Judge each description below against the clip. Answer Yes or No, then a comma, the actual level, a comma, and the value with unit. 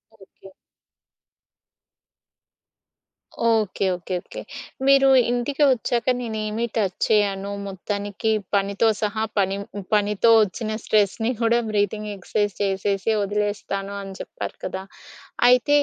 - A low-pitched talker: No, high, 205 Hz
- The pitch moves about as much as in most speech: No, narrow, 2.2 semitones